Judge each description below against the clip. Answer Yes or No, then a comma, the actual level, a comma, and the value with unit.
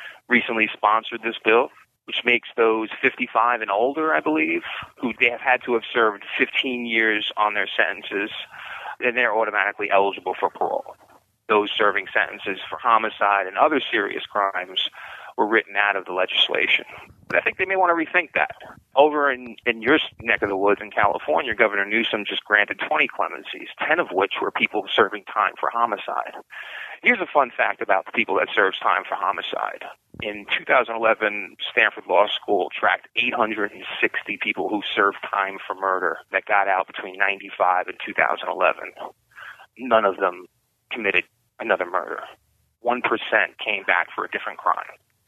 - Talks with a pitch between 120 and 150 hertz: No, low, 110 Hz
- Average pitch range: Yes, average, 3.4 semitones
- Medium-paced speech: Yes, average, 165 wpm